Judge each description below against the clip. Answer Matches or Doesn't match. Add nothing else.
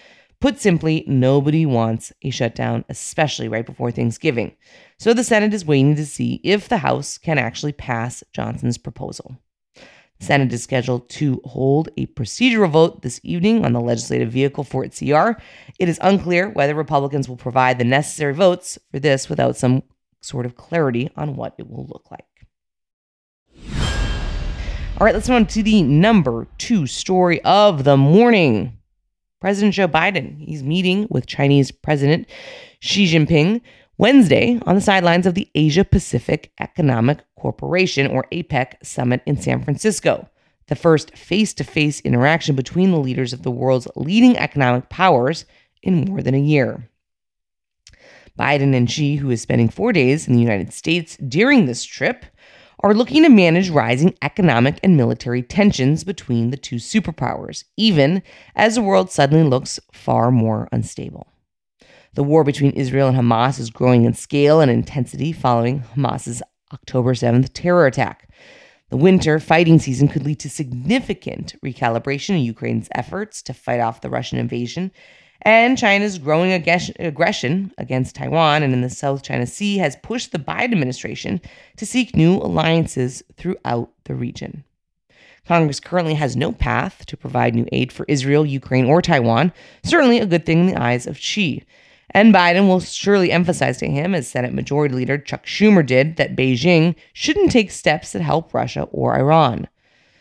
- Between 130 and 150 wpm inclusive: Doesn't match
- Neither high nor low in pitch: Matches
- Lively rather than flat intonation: Matches